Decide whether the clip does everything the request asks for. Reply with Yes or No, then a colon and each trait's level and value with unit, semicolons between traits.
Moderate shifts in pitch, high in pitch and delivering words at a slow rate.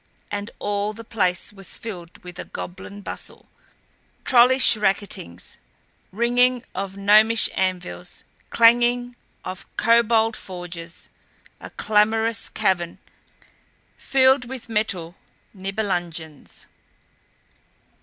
Yes: average, 4.1 semitones; high, 205 Hz; slow, 90 wpm